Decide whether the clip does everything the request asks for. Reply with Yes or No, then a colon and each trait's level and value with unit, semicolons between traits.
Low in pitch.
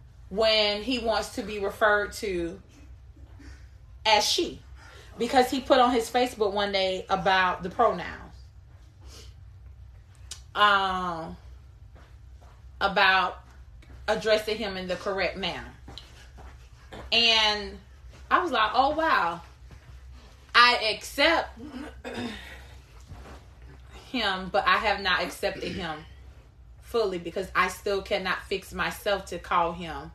No: high, 190 Hz